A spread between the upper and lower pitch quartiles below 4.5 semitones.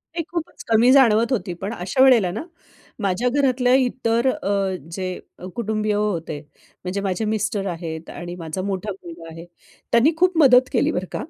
No: average, 5.3 semitones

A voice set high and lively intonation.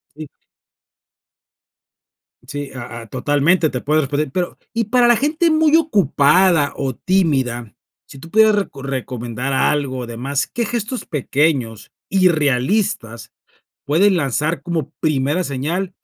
No: medium, 150 Hz; wide, 6.3 semitones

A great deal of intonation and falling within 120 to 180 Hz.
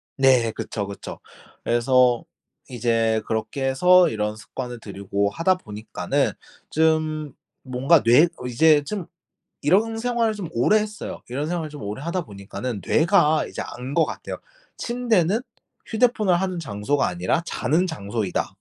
Yes: wide, 7.5 semitones; medium, 140 Hz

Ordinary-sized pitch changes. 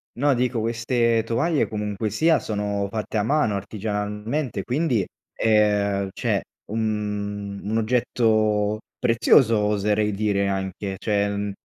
No: narrow, 2.1 semitones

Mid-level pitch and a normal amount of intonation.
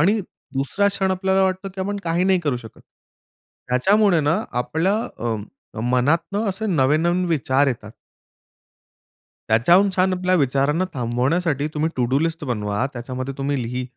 No: medium, 155 Hz; wide, 6.6 semitones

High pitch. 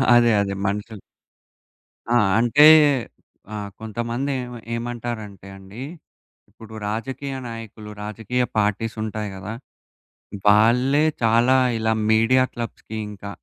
No: low, 115 Hz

